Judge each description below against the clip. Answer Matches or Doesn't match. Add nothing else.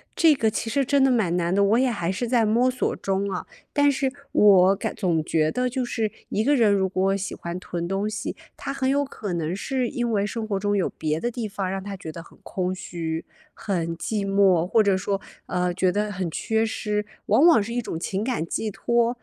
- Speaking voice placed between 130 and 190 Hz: Doesn't match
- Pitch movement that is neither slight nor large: Matches